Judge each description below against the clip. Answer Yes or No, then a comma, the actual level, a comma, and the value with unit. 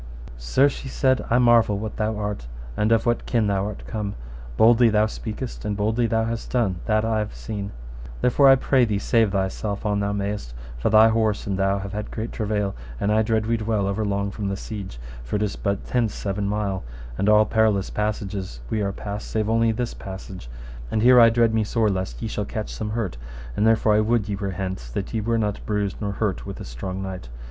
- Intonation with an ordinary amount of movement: No, narrow, 2.1 semitones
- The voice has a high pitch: No, low, 105 Hz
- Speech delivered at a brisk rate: Yes, fast, 225 wpm